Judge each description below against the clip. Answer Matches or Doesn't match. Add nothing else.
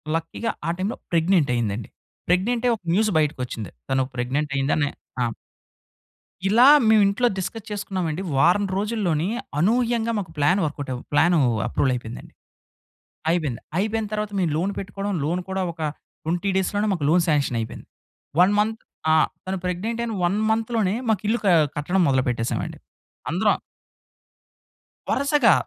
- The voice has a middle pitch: Matches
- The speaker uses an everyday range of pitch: Doesn't match